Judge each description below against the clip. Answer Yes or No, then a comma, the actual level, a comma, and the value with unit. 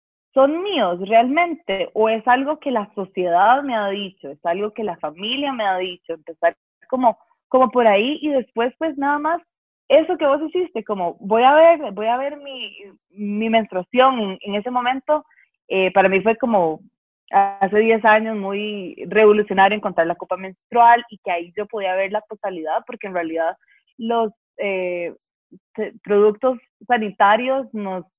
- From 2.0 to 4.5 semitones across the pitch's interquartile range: No, average, 4.9 semitones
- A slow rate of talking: No, average, 170 wpm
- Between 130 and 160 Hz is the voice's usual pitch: No, high, 215 Hz